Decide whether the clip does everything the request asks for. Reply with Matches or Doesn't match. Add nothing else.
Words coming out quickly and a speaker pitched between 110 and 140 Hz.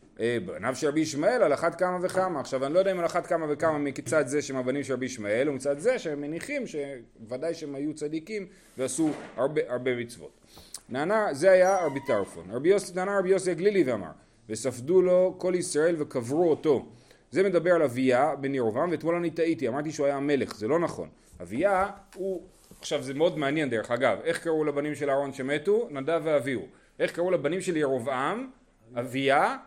Doesn't match